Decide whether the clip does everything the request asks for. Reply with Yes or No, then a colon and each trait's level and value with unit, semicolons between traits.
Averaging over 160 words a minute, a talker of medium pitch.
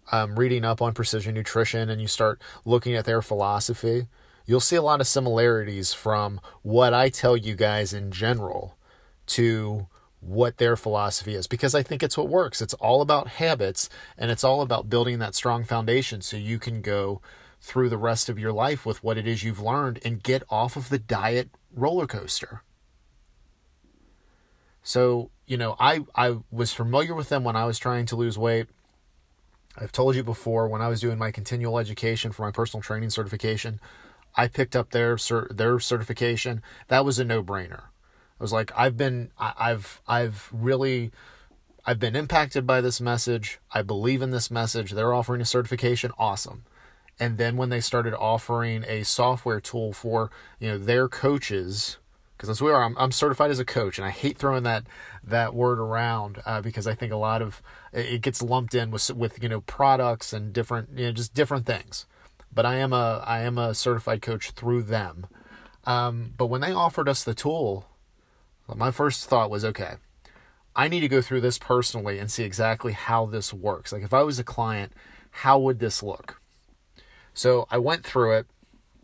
No: average, 190 wpm; low, 115 Hz